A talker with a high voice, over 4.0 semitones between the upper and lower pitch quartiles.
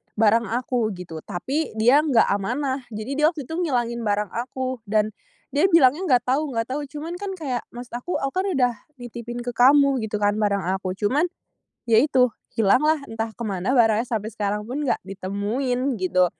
Yes: high, 240 Hz; average, 4.5 semitones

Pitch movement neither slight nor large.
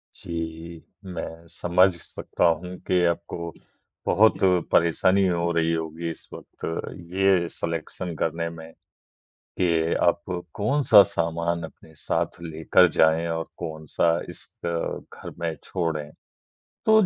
No: narrow, 1.7 semitones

